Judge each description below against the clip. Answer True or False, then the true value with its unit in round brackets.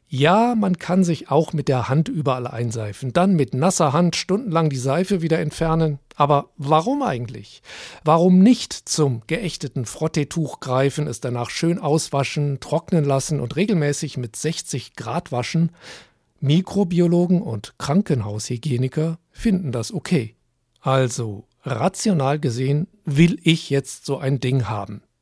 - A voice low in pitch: False (150 Hz)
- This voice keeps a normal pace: True (135 wpm)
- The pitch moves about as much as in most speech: True (4.6 semitones)